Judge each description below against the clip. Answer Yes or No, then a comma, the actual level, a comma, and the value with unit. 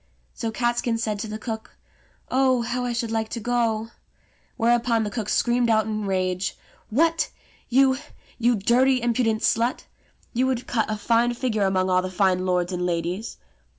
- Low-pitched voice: No, high, 225 Hz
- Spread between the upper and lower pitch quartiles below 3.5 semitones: Yes, average, 2.7 semitones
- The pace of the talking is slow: No, average, 175 wpm